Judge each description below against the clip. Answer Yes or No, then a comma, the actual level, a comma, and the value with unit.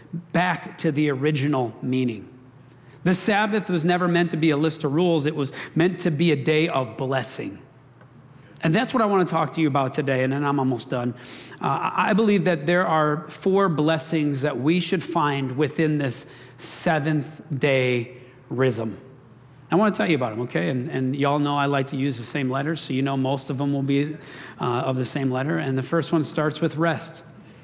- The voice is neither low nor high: Yes, medium, 145 Hz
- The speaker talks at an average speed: No, fast, 210 wpm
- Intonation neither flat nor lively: Yes, average, 3.8 semitones